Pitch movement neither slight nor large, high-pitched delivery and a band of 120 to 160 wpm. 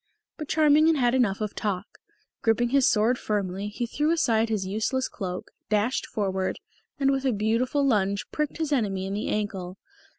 No: average, 4.9 semitones; high, 220 Hz; average, 175 wpm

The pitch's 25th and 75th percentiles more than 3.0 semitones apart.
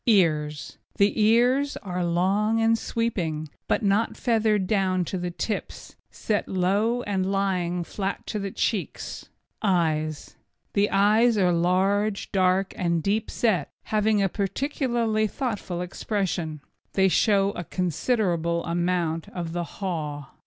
Yes: average, 3.6 semitones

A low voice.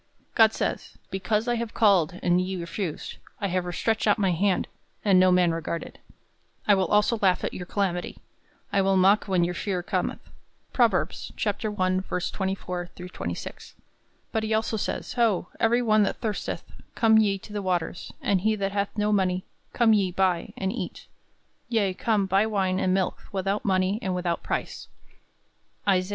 No: high, 195 Hz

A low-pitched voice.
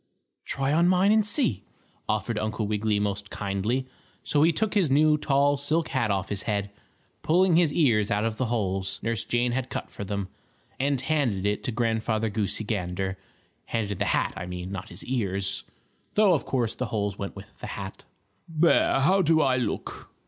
Yes: low, 115 Hz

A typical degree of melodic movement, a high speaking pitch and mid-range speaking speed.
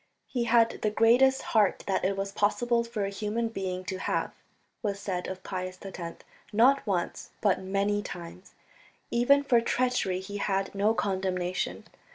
Yes: average, 3.5 semitones; high, 200 Hz; average, 160 wpm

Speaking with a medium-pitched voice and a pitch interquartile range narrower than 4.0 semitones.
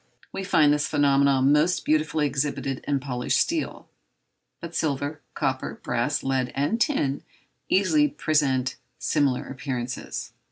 Yes: medium, 145 Hz; narrow, 2.4 semitones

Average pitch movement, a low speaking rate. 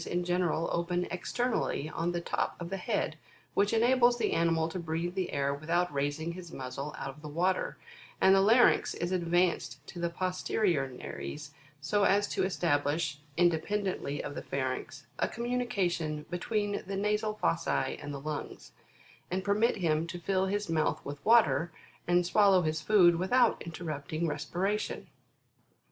No: average, 4.2 semitones; average, 160 wpm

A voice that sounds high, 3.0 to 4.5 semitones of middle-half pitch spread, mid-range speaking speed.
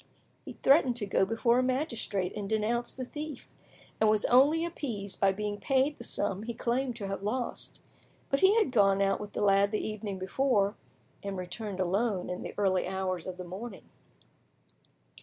Yes: high, 210 Hz; average, 4.2 semitones; average, 180 wpm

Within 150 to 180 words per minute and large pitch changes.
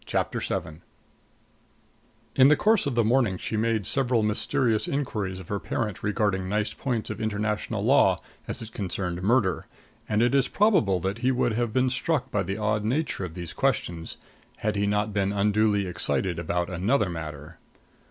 No: average, 170 wpm; average, 4.0 semitones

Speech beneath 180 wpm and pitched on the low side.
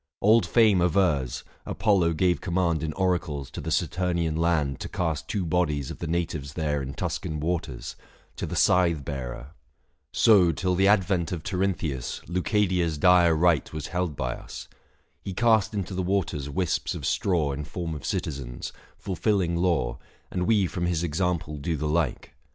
Yes: average, 170 wpm; very low, 85 Hz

